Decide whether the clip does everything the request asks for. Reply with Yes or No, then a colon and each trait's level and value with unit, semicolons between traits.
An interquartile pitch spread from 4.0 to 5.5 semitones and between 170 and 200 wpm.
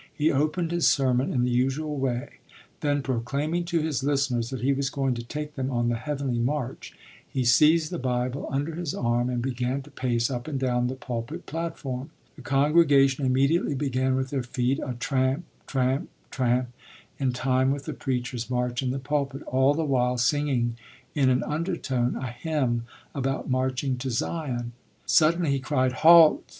No: average, 2.8 semitones; average, 175 wpm